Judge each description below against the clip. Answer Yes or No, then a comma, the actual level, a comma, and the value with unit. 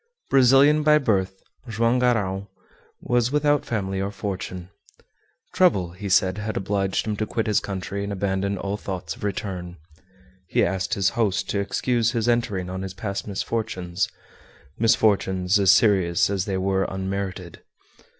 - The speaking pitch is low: Yes, low, 100 Hz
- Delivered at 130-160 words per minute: Yes, average, 150 wpm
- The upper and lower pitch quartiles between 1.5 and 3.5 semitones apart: Yes, average, 2.8 semitones